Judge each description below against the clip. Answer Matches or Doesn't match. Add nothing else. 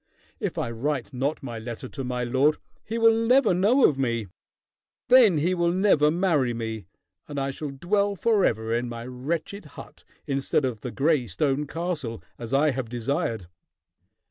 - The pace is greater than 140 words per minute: Matches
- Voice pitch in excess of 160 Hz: Doesn't match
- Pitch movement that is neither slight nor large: Doesn't match